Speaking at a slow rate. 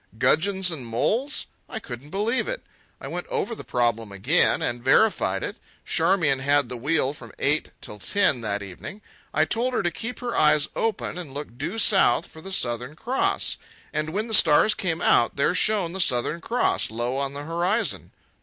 No: average, 185 wpm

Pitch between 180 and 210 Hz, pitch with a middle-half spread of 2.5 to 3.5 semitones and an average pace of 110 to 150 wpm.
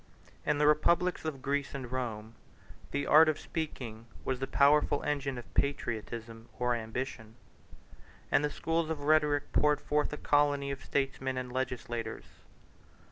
No: medium, 140 Hz; average, 3.2 semitones; average, 145 wpm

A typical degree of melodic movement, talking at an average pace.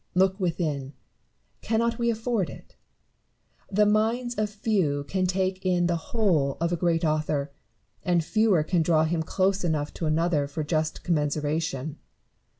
Yes: average, 4.3 semitones; average, 150 wpm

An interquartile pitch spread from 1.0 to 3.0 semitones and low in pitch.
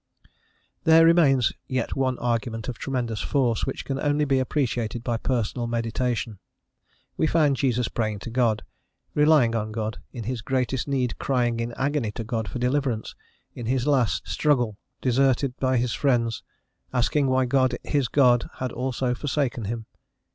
Yes: average, 2.7 semitones; low, 125 Hz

